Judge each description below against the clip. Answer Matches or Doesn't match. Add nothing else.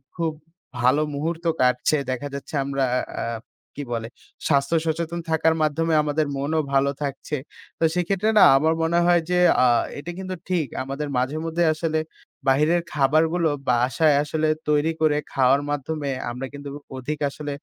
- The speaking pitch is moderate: Matches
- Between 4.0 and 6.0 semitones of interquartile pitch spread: Doesn't match